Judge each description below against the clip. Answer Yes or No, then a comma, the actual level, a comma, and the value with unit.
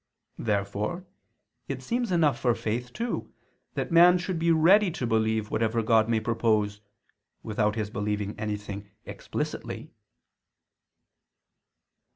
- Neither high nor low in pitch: No, low, 115 Hz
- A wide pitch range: Yes, wide, 7.7 semitones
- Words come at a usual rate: No, slow, 115 wpm